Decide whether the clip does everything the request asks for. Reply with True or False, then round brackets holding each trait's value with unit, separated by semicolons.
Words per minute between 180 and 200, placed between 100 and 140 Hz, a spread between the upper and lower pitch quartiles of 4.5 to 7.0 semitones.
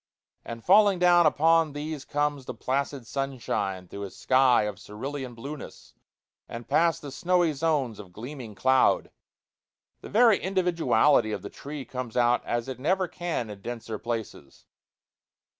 False (145 wpm; 135 Hz; 5.4 semitones)